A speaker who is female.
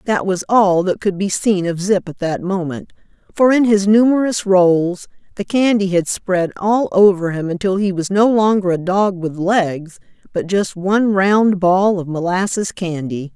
Yes: female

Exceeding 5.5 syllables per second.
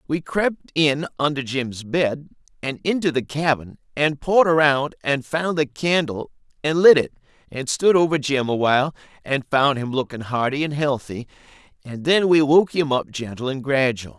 No: 4.8 syllables/s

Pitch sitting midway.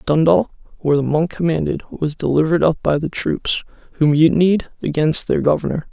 Yes: medium, 160 Hz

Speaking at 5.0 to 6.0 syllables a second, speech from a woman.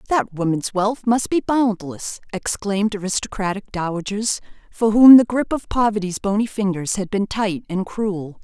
No: 4.7 syllables/s; female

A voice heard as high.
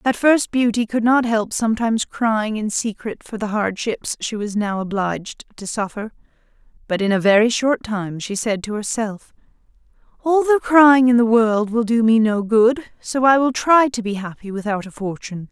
Yes: high, 225 Hz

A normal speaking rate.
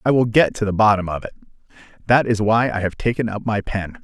No: fast, 255 wpm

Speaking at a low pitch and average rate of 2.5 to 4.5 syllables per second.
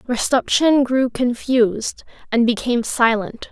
No: high, 245 Hz; 4.2 syllables/s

